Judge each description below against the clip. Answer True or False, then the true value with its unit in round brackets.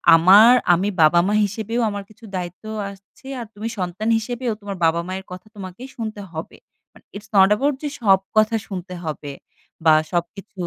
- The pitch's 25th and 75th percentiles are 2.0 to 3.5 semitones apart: True (3.2 semitones)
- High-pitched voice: True (200 Hz)